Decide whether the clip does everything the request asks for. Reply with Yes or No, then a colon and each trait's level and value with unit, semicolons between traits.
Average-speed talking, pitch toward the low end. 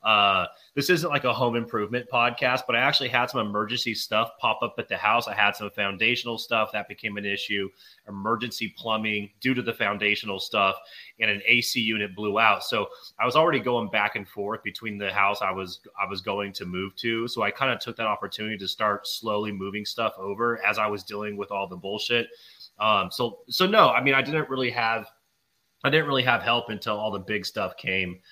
No: fast, 220 wpm; low, 110 Hz